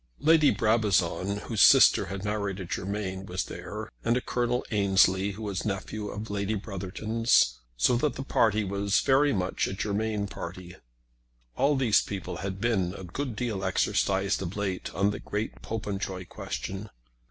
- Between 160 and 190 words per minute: Yes, average, 165 wpm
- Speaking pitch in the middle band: No, low, 100 Hz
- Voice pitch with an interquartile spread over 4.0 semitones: No, narrow, 2.6 semitones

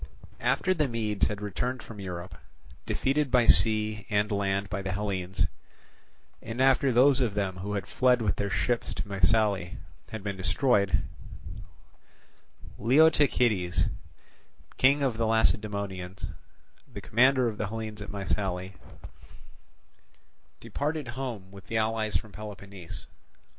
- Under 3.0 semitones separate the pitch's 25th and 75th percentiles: No, average, 3.7 semitones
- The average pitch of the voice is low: Yes, low, 105 Hz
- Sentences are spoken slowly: Yes, slow, 125 wpm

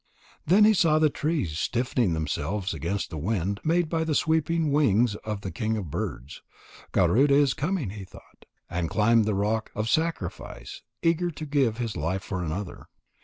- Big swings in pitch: Yes, wide, 8.0 semitones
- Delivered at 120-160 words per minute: No, average, 170 wpm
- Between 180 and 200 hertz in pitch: No, low, 115 Hz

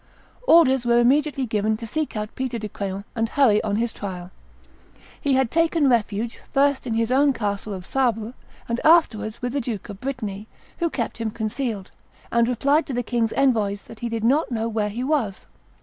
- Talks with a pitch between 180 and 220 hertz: No, high, 235 Hz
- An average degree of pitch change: Yes, average, 3.8 semitones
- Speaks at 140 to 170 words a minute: No, average, 195 wpm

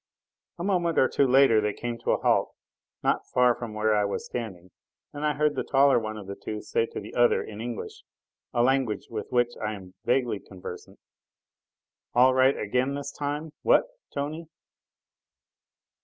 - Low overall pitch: Yes, low, 120 Hz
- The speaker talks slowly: No, average, 175 wpm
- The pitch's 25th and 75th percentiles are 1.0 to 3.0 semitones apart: No, average, 4.6 semitones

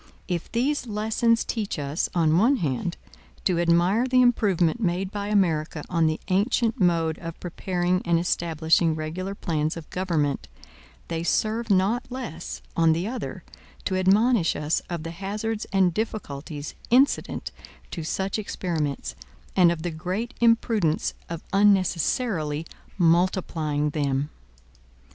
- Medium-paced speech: No, slow, 130 wpm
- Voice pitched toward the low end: No, medium, 180 Hz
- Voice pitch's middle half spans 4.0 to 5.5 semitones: Yes, average, 4.6 semitones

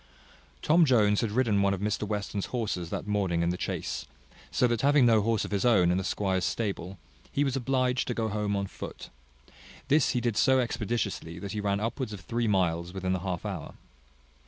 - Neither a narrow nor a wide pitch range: Yes, average, 3.9 semitones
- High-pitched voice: No, low, 105 Hz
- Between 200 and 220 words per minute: Yes, fast, 205 wpm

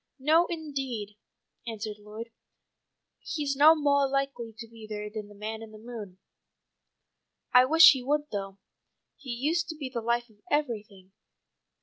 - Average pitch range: Yes, average, 5.0 semitones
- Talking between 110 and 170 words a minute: Yes, average, 150 wpm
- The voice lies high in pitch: Yes, high, 240 Hz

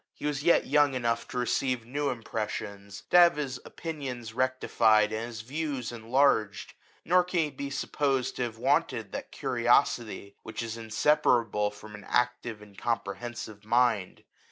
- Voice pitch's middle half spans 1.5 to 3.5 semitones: No, average, 4.1 semitones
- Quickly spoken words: No, average, 155 wpm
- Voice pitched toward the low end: Yes, low, 120 Hz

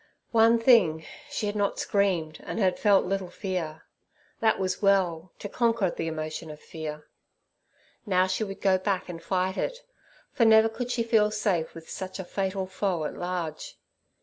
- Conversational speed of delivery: Yes, average, 175 wpm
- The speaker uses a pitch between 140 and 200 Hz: Yes, high, 190 Hz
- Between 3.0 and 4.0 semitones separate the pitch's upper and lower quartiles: Yes, average, 3.7 semitones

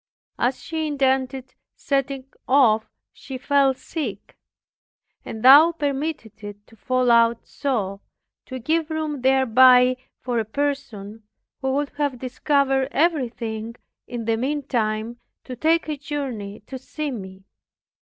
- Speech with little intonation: No, average, 3.8 semitones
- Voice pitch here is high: Yes, very high, 260 Hz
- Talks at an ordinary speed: No, slow, 125 wpm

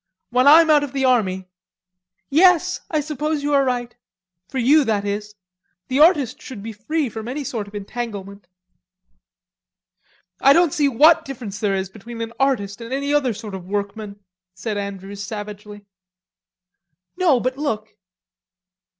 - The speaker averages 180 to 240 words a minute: No, average, 150 wpm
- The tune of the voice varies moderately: No, wide, 5.7 semitones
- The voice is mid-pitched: No, high, 235 Hz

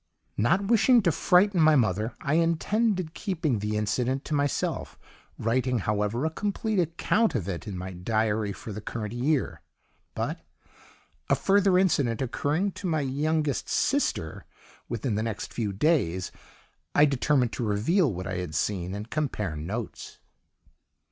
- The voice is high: No, low, 130 Hz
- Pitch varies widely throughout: Yes, wide, 7.6 semitones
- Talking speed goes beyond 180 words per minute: No, average, 150 wpm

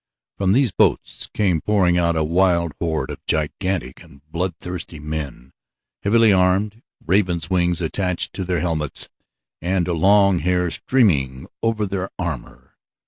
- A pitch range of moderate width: Yes, average, 3.3 semitones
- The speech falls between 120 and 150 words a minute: Yes, slow, 135 wpm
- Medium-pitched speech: No, very low, 90 Hz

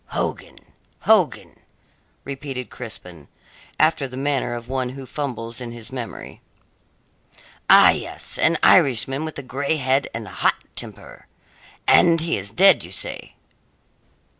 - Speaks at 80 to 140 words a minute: Yes, slow, 135 wpm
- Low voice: Yes, low, 130 Hz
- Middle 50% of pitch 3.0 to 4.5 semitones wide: Yes, average, 3.3 semitones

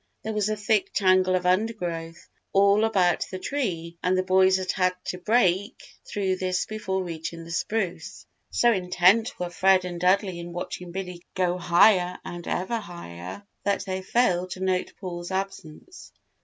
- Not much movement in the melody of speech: Yes, narrow, 2.2 semitones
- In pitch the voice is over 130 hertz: Yes, medium, 185 Hz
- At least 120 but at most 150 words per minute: No, average, 165 wpm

